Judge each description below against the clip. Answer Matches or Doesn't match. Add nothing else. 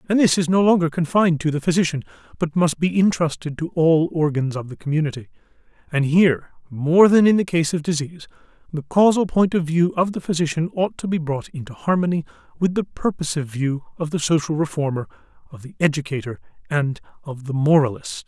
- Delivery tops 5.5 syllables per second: Matches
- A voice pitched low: Doesn't match